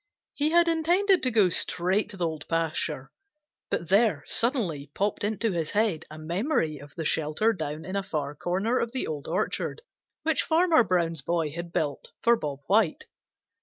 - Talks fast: No, average, 175 wpm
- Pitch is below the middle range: No, medium, 180 Hz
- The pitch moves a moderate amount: No, wide, 6.5 semitones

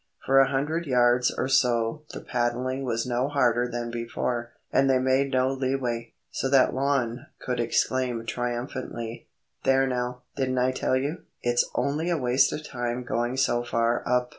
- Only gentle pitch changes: Yes, narrow, 1.8 semitones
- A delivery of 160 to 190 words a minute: Yes, average, 165 wpm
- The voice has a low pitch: Yes, low, 125 Hz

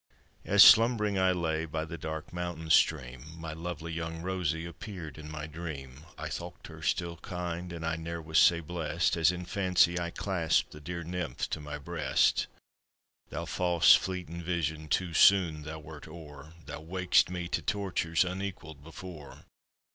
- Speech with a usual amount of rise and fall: No, narrow, 2.2 semitones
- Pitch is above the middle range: No, very low, 85 Hz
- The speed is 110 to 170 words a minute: Yes, average, 165 wpm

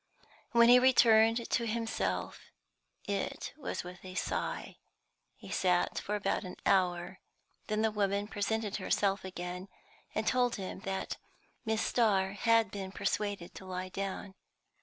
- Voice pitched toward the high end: Yes, high, 200 Hz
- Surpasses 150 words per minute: No, average, 140 wpm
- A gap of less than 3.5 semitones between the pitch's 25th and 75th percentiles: Yes, average, 2.8 semitones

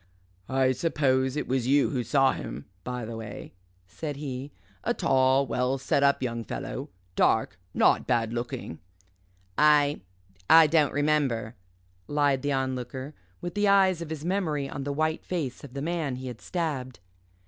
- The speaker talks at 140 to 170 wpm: Yes, average, 160 wpm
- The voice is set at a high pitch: No, low, 135 Hz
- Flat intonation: No, average, 3.1 semitones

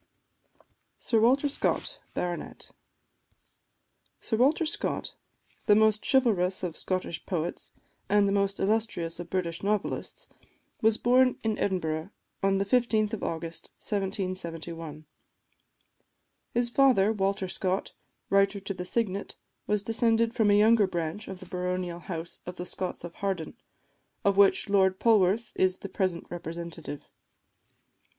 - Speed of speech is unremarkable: No, slow, 130 wpm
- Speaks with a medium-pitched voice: No, high, 195 Hz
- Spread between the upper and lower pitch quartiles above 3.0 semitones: Yes, average, 3.5 semitones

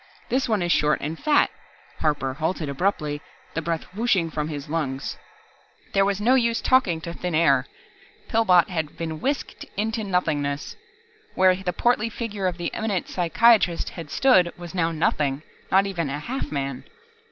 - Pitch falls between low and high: Yes, medium, 175 Hz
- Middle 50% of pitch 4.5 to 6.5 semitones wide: Yes, average, 5.1 semitones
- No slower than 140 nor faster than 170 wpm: Yes, average, 165 wpm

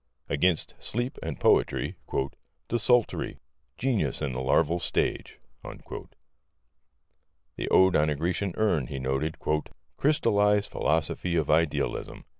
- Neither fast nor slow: No, slow, 105 wpm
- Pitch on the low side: Yes, very low, 85 Hz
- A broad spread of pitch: Yes, wide, 5.7 semitones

